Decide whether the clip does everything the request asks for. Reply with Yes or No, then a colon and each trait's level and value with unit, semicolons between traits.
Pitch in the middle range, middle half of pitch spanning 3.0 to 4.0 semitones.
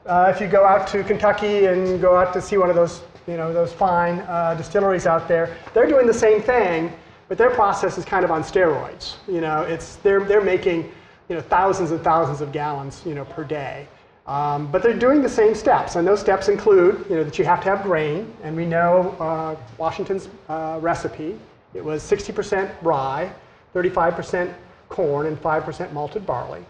Yes: medium, 180 Hz; average, 3.4 semitones